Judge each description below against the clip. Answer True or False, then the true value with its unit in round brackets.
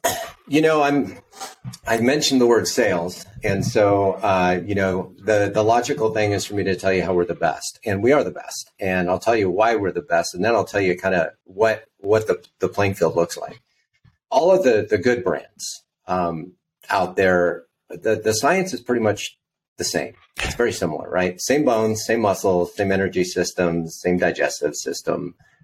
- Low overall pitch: True (100 Hz)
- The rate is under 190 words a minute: False (200 wpm)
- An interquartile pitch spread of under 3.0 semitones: False (3.3 semitones)